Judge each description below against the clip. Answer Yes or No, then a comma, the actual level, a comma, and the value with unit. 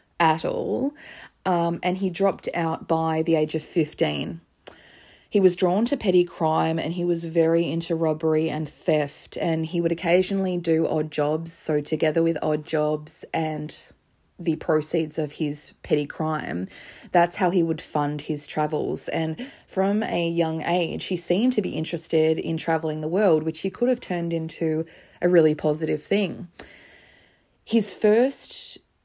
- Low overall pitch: No, medium, 165 Hz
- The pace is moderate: Yes, average, 160 wpm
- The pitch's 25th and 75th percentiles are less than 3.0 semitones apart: Yes, narrow, 2.4 semitones